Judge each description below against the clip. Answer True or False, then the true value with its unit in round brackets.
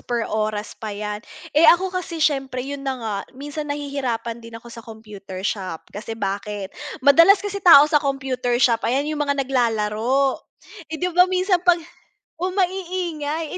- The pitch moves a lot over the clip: True (6.3 semitones)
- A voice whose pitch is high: True (270 Hz)